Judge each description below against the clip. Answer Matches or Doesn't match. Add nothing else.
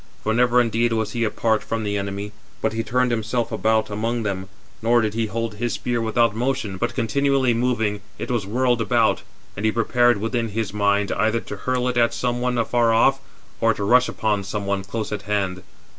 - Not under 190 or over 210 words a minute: Matches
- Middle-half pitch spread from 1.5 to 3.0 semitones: Matches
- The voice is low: Matches